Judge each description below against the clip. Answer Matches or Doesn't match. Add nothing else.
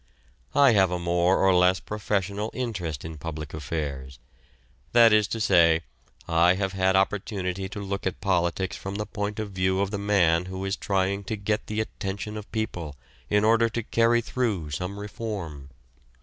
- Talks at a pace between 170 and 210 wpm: Matches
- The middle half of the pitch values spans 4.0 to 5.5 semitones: Doesn't match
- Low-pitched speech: Matches